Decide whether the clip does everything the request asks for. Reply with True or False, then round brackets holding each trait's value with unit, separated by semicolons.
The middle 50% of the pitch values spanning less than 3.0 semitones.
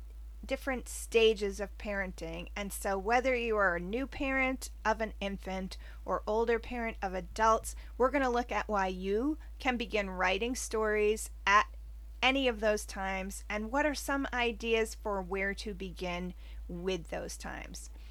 False (4.0 semitones)